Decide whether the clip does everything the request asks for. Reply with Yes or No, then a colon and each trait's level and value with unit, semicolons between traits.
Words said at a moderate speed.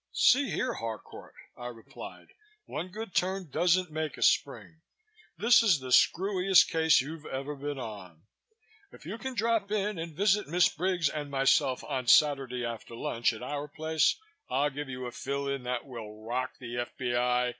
Yes: average, 170 wpm